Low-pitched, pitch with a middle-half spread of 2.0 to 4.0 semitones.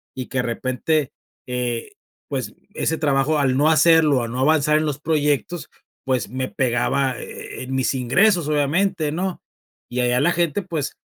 No: medium, 145 Hz; average, 3.7 semitones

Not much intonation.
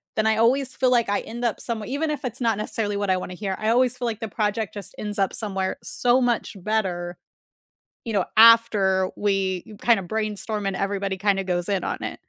No: average, 3.0 semitones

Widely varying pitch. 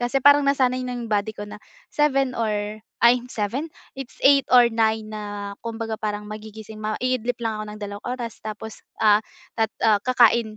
No: average, 2.9 semitones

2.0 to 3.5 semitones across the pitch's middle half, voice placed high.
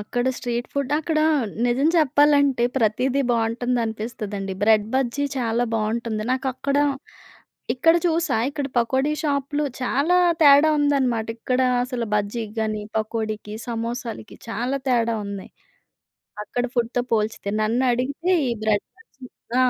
No: average, 3.9 semitones; high, 245 Hz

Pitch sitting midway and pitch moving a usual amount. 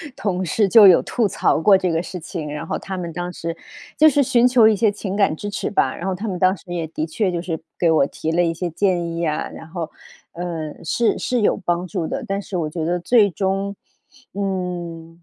Yes: medium, 180 Hz; average, 3.2 semitones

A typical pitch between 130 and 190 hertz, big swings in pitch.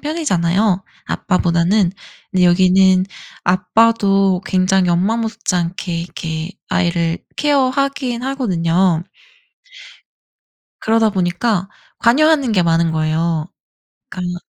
No: medium, 185 Hz; average, 4.7 semitones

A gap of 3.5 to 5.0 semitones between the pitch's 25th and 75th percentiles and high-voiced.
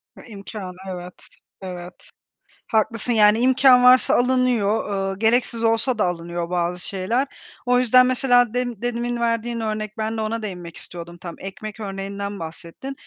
Yes: average, 4.3 semitones; high, 220 Hz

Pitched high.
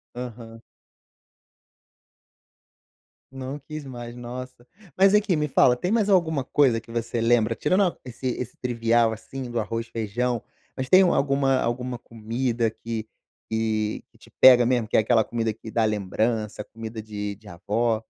No: low, 120 Hz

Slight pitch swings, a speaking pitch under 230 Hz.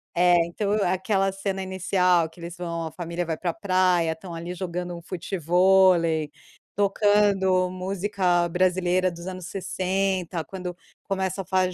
Yes: narrow, 1.7 semitones; medium, 185 Hz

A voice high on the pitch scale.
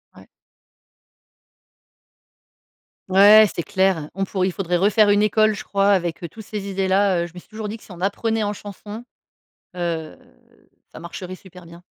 Yes: high, 195 Hz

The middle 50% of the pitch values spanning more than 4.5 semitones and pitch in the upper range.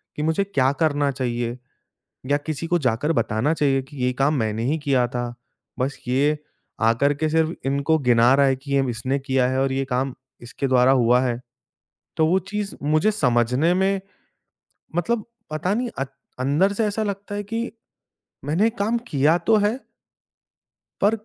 No: average, 5.3 semitones; medium, 140 Hz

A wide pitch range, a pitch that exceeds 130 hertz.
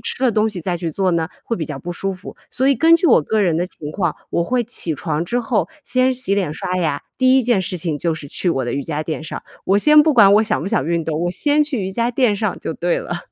Yes: wide, 6.8 semitones; medium, 185 Hz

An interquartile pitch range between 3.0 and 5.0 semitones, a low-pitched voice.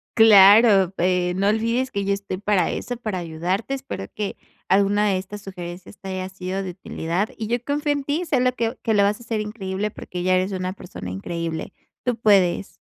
No: average, 3.3 semitones; high, 200 Hz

